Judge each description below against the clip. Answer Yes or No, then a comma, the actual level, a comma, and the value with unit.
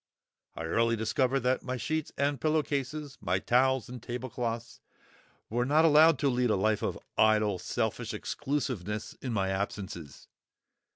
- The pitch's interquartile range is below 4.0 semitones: No, average, 4.3 semitones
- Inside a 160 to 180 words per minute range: No, average, 150 wpm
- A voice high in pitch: No, low, 125 Hz